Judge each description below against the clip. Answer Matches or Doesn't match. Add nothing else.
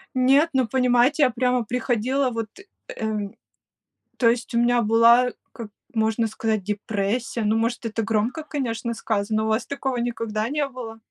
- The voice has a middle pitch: Doesn't match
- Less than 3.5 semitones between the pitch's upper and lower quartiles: Matches